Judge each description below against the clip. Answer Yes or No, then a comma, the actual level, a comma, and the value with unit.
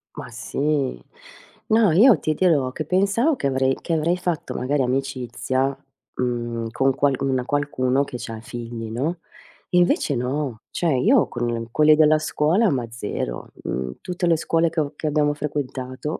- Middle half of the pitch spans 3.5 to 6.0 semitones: Yes, average, 4.1 semitones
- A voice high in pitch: No, medium, 140 Hz